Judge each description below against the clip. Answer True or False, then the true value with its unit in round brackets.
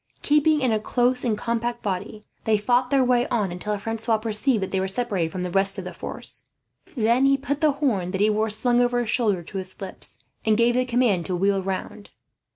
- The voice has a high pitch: True (220 Hz)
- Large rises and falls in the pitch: False (4.0 semitones)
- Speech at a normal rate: False (225 wpm)